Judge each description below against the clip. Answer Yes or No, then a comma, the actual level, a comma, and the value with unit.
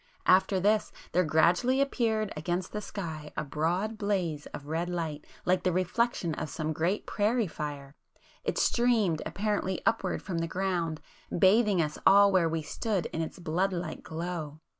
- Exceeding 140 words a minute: Yes, average, 160 wpm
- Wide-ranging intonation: No, average, 4.2 semitones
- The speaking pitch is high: No, medium, 180 Hz